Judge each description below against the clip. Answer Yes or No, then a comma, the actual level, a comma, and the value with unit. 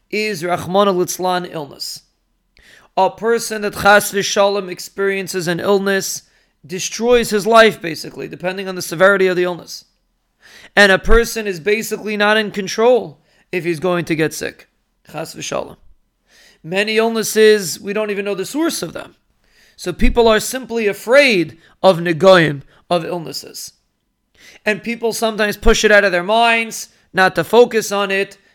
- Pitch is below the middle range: No, high, 200 Hz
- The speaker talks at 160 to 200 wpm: No, average, 150 wpm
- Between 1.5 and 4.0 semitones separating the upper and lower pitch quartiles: Yes, average, 3.3 semitones